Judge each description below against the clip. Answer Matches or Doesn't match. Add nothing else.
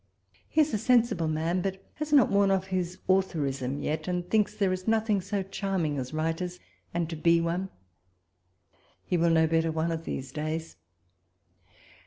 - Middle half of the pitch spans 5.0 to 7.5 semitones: Doesn't match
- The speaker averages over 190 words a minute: Doesn't match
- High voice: Doesn't match